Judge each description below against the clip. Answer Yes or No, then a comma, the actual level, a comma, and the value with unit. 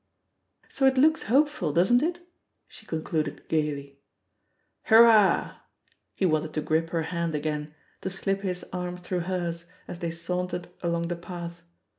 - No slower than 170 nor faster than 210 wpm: No, average, 155 wpm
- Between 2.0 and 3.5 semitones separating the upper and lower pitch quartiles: Yes, average, 3.1 semitones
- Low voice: No, medium, 175 Hz